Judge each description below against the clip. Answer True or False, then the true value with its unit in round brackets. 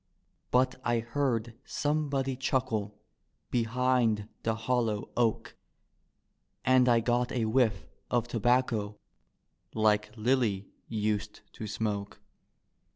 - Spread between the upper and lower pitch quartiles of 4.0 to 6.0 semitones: False (2.9 semitones)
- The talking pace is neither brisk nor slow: False (95 wpm)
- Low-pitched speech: True (115 Hz)